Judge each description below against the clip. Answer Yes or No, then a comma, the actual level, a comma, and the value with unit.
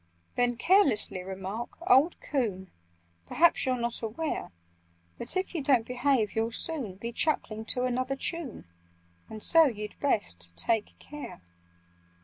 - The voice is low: No, high, 240 Hz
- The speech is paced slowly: Yes, slow, 130 wpm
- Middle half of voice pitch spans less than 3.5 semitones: No, average, 4.9 semitones